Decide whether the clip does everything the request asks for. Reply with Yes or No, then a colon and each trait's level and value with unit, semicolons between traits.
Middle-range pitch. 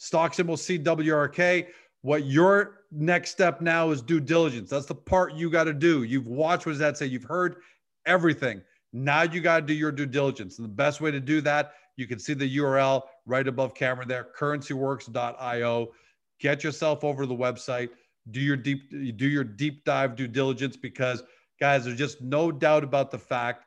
Yes: medium, 145 Hz